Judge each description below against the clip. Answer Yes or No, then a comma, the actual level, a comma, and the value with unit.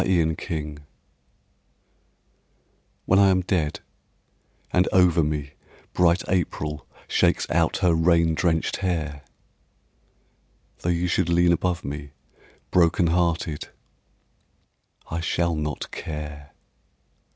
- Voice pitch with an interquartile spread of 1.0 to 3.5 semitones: Yes, narrow, 2.6 semitones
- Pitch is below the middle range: Yes, very low, 85 Hz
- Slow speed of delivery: Yes, slow, 105 wpm